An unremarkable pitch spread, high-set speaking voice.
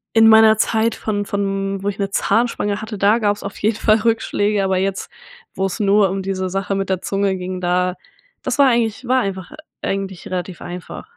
No: narrow, 2.2 semitones; high, 200 Hz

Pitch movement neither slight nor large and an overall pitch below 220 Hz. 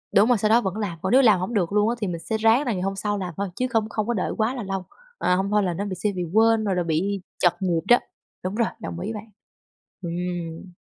Yes: average, 3.4 semitones; high, 200 Hz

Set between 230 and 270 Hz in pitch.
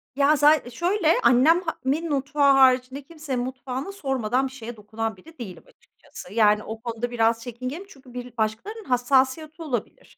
Yes: very high, 260 Hz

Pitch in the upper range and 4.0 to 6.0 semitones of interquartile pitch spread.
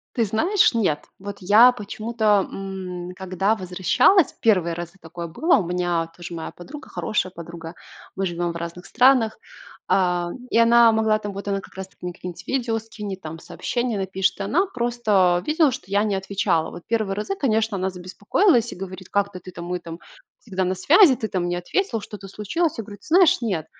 Yes: high, 195 Hz; average, 4.3 semitones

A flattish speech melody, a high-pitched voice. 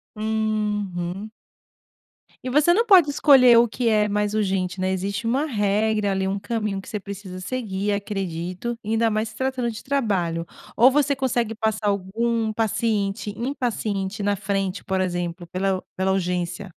No: average, 3.3 semitones; high, 210 Hz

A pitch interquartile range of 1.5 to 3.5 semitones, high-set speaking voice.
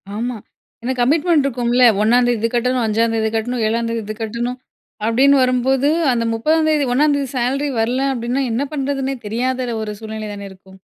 Yes: average, 2.9 semitones; high, 245 Hz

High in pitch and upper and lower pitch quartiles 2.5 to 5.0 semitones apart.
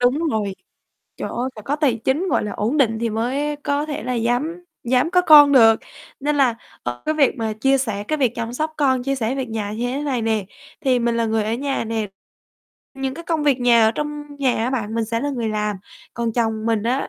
Yes: high, 245 Hz; average, 4.2 semitones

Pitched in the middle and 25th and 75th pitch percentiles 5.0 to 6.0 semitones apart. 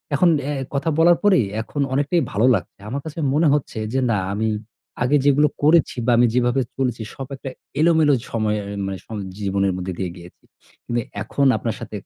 No: low, 130 Hz; wide, 5.4 semitones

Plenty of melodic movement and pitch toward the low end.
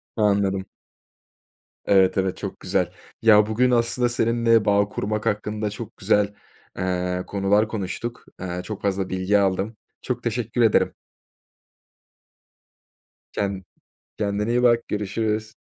No: average, 2.7 semitones; low, 105 Hz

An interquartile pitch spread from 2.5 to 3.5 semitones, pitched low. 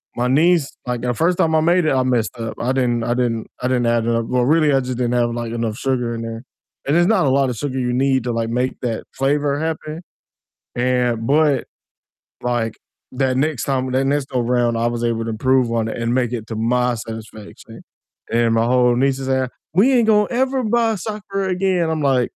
No: average, 3.9 semitones; low, 125 Hz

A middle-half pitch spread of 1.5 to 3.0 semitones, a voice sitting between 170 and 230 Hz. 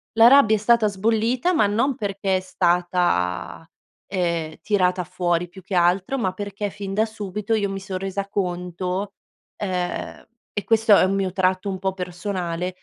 Yes: narrow, 2.5 semitones; high, 190 Hz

